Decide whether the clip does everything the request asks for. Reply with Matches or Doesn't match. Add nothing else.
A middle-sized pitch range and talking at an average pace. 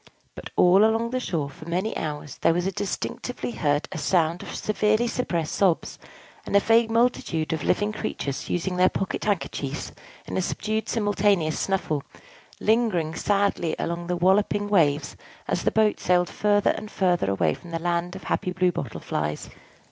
Matches